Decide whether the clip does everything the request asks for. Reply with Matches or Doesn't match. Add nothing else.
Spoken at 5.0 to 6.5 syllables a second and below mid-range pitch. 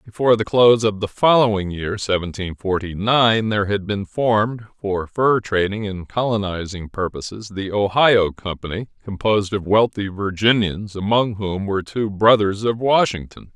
Doesn't match